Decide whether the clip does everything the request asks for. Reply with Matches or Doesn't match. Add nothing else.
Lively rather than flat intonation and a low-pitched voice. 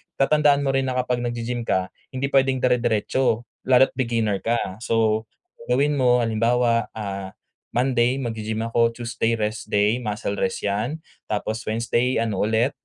Doesn't match